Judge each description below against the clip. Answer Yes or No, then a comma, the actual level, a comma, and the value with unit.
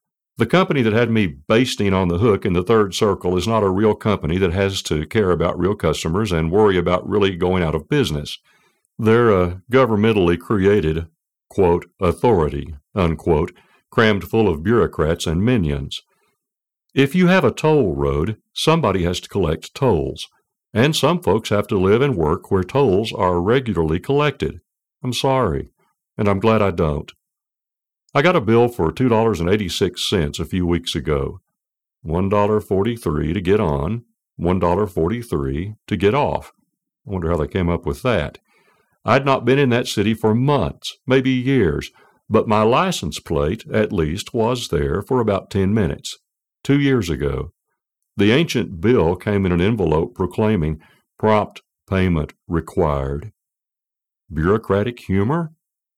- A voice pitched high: No, low, 100 Hz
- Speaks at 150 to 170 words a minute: Yes, average, 160 wpm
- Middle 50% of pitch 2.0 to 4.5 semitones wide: No, average, 5.0 semitones